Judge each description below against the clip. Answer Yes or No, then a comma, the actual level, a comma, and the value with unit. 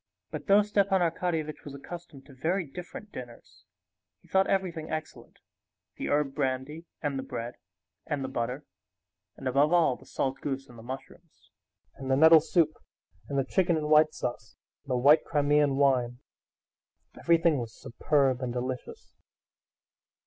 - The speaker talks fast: No, average, 150 wpm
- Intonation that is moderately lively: Yes, average, 3.8 semitones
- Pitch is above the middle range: No, medium, 145 Hz